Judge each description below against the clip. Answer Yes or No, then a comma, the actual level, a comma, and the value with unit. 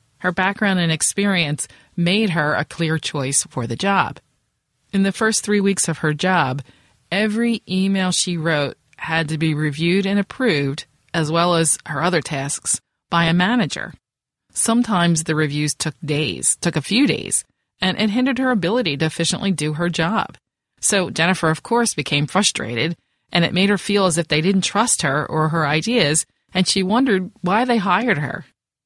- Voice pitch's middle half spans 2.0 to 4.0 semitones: No, average, 4.5 semitones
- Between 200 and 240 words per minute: No, average, 175 wpm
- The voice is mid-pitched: Yes, medium, 175 Hz